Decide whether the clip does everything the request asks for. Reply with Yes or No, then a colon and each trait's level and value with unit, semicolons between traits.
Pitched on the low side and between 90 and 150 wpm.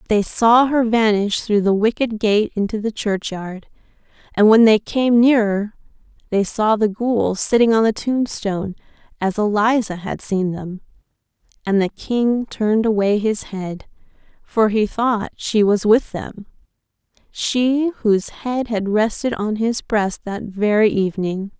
No: high, 215 Hz; average, 145 wpm